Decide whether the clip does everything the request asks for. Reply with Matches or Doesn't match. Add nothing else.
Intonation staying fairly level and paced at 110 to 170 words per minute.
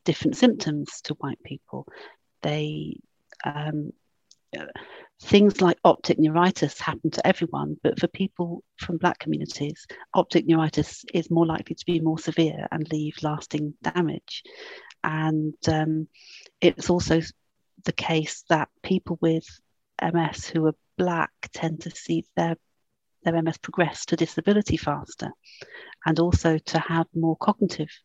Matches